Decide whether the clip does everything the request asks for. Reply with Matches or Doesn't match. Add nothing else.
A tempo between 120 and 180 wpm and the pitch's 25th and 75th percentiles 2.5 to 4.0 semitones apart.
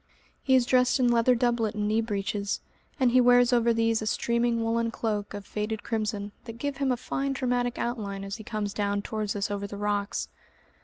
Doesn't match